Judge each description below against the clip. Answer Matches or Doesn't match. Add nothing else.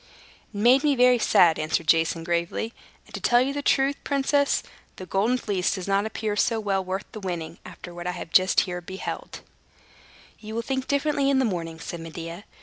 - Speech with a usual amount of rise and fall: Doesn't match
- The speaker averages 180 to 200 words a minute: Matches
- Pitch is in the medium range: Doesn't match